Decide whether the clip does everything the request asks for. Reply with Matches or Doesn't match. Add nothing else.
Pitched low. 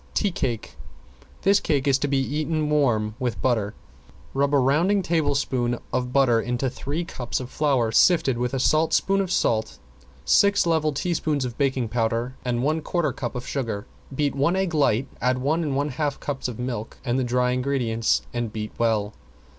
Matches